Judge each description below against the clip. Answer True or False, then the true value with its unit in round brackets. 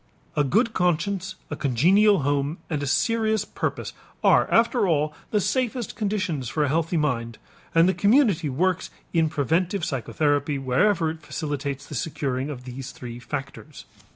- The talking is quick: False (155 wpm)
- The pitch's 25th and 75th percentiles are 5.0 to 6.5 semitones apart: True (5.5 semitones)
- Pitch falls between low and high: True (155 Hz)